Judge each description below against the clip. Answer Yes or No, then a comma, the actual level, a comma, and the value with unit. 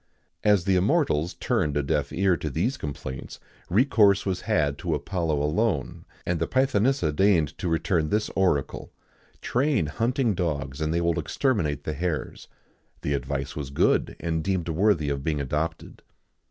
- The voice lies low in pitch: Yes, very low, 85 Hz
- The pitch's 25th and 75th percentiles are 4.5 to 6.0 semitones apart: Yes, average, 5.2 semitones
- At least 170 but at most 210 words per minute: No, average, 160 wpm